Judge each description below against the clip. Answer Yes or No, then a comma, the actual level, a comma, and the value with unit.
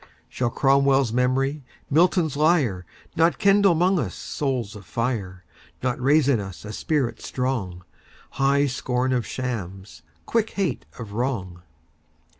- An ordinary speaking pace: No, slow, 115 wpm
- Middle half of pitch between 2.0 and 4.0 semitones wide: No, wide, 5.5 semitones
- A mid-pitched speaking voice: No, low, 130 Hz